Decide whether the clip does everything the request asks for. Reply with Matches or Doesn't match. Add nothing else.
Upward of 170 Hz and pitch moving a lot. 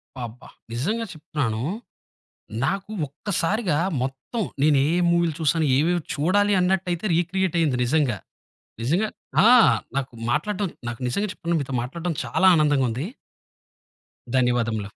Doesn't match